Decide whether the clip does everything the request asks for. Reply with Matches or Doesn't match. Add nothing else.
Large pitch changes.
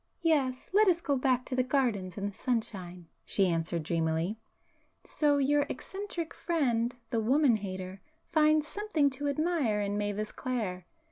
Matches